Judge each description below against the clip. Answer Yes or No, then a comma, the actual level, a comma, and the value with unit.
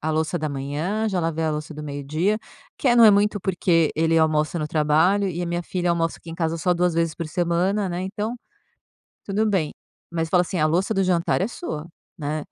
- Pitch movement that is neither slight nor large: Yes, average, 3.4 semitones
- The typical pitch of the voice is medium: Yes, medium, 170 Hz